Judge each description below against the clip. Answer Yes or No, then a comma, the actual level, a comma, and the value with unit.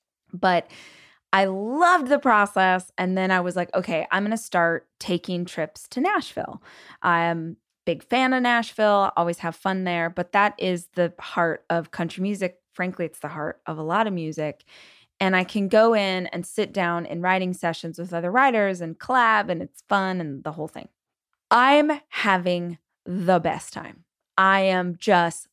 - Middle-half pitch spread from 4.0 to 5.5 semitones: No, average, 3.2 semitones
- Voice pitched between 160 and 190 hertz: Yes, medium, 185 Hz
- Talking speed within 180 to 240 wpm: Yes, average, 185 wpm